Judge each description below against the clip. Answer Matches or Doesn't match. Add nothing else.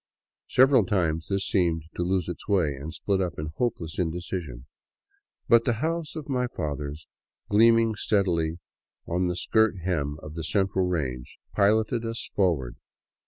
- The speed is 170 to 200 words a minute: Doesn't match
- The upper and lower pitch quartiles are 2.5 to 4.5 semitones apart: Doesn't match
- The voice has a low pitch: Matches